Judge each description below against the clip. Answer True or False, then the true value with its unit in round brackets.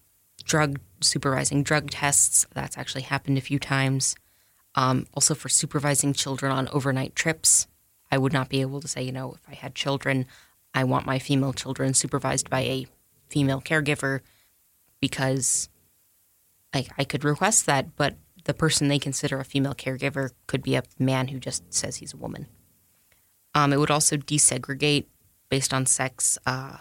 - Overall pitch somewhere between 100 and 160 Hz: True (135 Hz)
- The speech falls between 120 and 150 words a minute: False (165 wpm)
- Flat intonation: True (1.8 semitones)